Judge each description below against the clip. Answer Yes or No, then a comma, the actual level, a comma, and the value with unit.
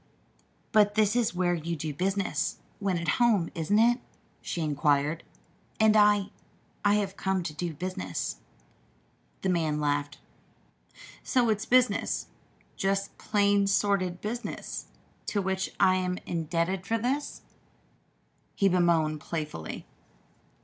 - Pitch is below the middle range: No, medium, 185 Hz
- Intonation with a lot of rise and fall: No, average, 4.1 semitones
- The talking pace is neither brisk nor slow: No, slow, 120 wpm